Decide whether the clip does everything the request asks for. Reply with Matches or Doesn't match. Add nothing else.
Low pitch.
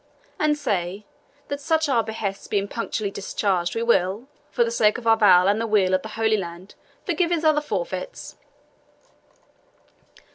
Doesn't match